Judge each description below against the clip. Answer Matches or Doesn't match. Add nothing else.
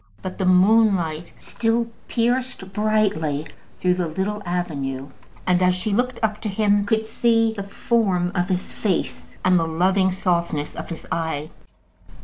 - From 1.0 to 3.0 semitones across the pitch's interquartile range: Doesn't match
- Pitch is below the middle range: Doesn't match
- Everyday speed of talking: Matches